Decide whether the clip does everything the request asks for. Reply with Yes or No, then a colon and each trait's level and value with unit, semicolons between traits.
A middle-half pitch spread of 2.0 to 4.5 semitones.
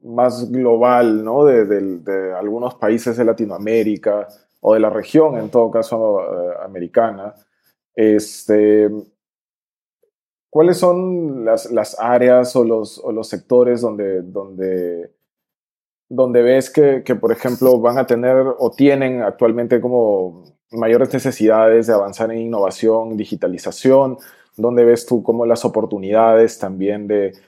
Yes: average, 3.0 semitones